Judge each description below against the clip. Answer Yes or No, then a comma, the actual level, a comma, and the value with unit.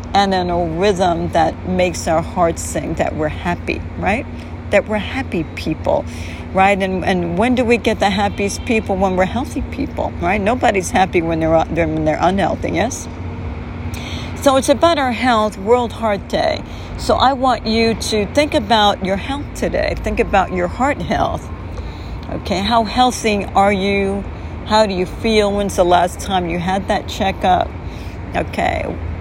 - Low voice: No, high, 190 Hz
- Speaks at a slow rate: No, average, 165 wpm